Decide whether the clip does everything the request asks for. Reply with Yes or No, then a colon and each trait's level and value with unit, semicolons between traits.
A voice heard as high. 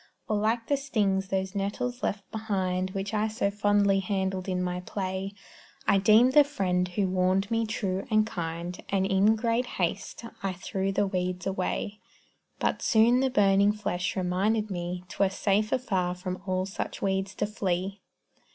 Yes: high, 195 Hz